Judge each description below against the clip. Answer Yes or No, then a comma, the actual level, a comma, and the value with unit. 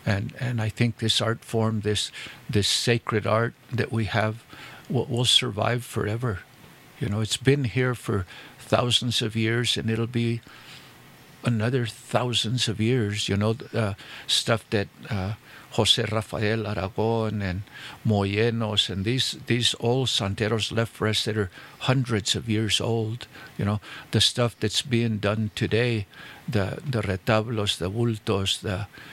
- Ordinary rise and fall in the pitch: No, narrow, 2.1 semitones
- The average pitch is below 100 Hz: No, low, 110 Hz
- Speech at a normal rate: Yes, average, 150 wpm